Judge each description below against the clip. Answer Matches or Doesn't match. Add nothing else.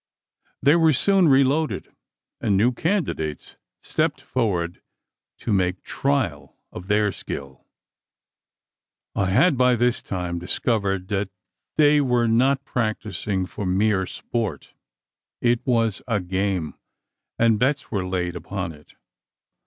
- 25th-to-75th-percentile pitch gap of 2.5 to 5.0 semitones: Doesn't match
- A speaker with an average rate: Doesn't match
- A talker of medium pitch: Doesn't match